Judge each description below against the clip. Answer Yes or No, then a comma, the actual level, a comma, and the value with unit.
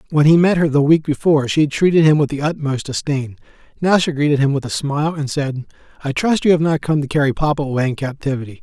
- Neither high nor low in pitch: Yes, medium, 145 Hz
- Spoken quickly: Yes, fast, 245 wpm